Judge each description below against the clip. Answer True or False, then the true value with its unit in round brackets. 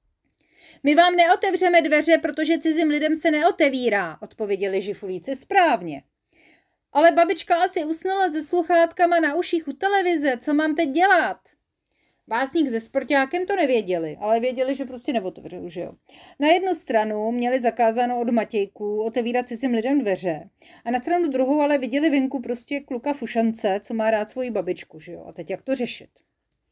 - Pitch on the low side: False (280 Hz)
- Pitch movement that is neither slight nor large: False (6.6 semitones)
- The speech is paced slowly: False (160 wpm)